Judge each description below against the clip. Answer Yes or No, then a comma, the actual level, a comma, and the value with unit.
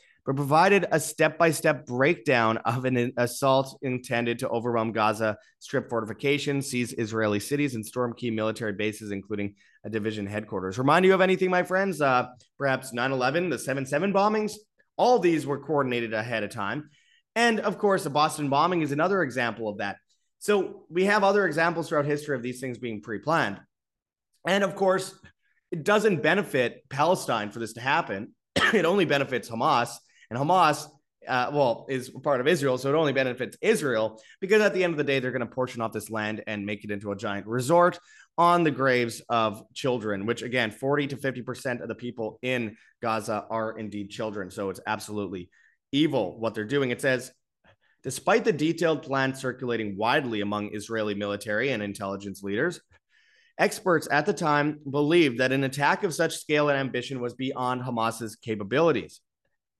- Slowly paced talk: No, average, 180 wpm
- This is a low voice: Yes, low, 130 Hz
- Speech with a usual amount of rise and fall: No, wide, 6.3 semitones